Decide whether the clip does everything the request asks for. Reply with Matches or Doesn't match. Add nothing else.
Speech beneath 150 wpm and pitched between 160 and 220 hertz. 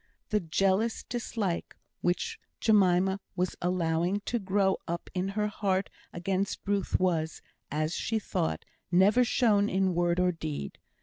Matches